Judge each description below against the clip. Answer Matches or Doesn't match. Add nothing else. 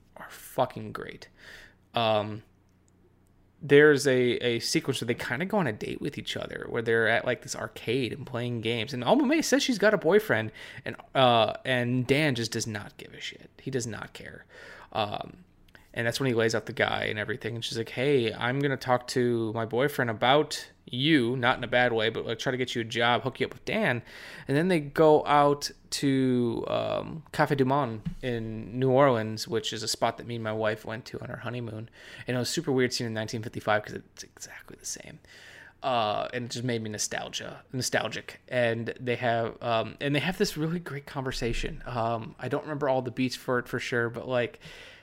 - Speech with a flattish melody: Doesn't match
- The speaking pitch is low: Matches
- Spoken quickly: Matches